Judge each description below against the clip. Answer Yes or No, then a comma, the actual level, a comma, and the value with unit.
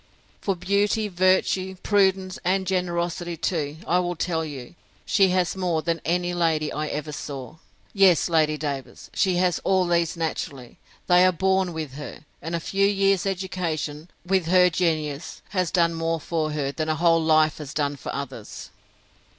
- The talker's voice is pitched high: No, medium, 170 Hz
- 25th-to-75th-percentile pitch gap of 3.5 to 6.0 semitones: No, average, 3.0 semitones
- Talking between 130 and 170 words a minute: Yes, average, 165 wpm